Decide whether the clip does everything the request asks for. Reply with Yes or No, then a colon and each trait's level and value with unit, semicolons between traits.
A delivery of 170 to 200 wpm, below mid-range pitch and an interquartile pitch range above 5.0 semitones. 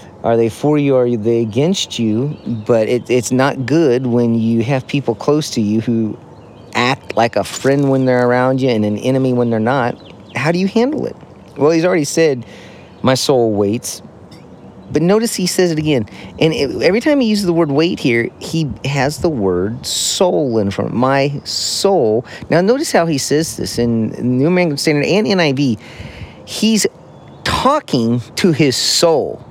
Yes: average, 180 wpm; low, 130 Hz; wide, 5.5 semitones